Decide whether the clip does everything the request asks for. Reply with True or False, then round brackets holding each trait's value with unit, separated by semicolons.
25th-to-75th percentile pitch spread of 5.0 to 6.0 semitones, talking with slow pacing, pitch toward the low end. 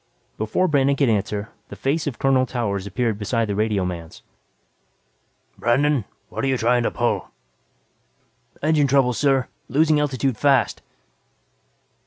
False (4.4 semitones; 125 wpm; 125 Hz)